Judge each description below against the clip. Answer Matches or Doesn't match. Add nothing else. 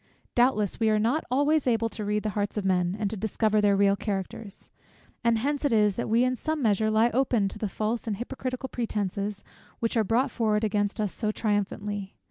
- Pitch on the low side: Doesn't match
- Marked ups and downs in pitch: Doesn't match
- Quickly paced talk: Matches